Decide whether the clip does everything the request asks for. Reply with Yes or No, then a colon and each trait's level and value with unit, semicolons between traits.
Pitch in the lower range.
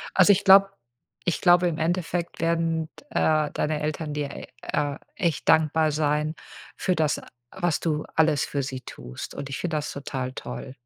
No: medium, 155 Hz